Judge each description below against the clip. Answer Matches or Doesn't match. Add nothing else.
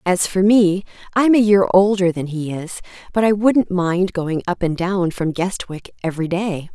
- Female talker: Matches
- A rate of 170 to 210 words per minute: Matches